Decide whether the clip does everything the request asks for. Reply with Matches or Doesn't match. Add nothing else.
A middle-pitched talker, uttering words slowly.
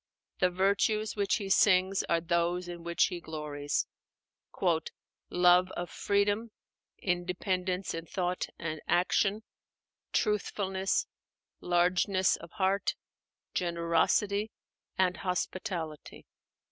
Matches